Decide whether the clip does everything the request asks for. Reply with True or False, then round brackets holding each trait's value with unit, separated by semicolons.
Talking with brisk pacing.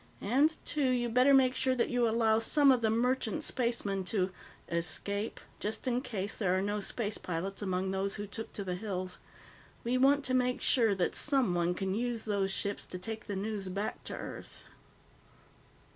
False (185 wpm)